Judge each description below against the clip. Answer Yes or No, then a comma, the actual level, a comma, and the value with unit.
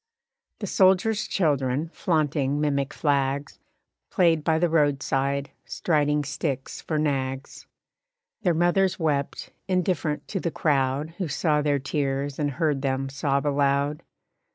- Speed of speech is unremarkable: No, slow, 125 wpm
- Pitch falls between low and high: Yes, medium, 145 Hz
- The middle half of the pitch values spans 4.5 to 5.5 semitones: No, average, 2.8 semitones